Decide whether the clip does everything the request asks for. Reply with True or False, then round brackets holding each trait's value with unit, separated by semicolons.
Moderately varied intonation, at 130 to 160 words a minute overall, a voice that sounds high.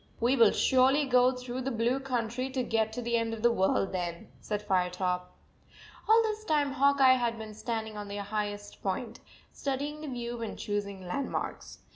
False (4.1 semitones; 195 wpm; 235 Hz)